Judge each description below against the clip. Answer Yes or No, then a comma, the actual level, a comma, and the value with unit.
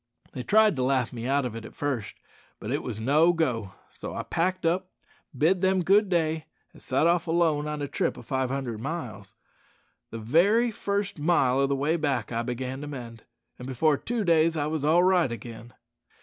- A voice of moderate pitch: Yes, medium, 145 Hz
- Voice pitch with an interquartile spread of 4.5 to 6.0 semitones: Yes, wide, 5.4 semitones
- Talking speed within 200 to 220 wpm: Yes, fast, 205 wpm